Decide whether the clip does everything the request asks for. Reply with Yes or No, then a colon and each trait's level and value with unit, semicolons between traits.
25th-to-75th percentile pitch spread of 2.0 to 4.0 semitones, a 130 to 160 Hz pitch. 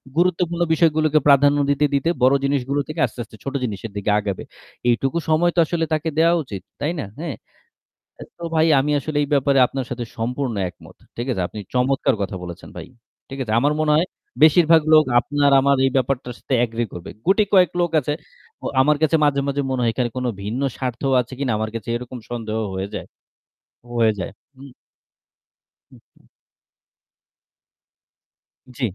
No: average, 4.4 semitones; low, 135 Hz